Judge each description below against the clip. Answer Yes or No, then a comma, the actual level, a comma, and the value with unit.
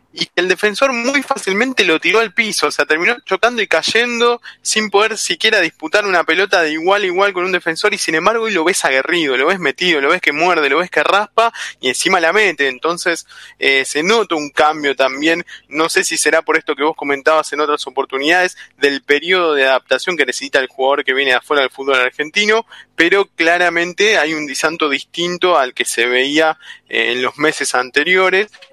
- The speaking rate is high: Yes, fast, 210 wpm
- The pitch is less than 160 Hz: No, medium, 175 Hz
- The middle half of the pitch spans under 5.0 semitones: No, wide, 5.5 semitones